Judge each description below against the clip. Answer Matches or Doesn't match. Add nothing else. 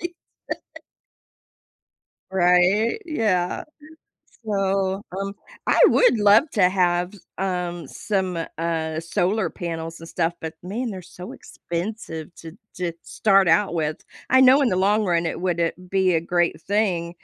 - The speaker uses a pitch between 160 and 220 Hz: Matches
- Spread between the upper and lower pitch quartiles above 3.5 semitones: Doesn't match